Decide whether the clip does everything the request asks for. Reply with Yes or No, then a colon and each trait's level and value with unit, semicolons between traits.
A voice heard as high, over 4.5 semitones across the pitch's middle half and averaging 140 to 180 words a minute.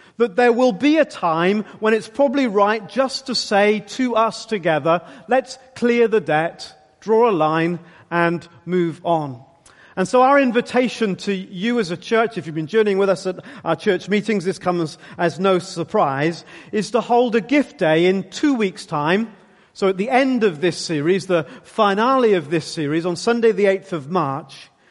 No: high, 195 Hz; average, 5.2 semitones; average, 190 wpm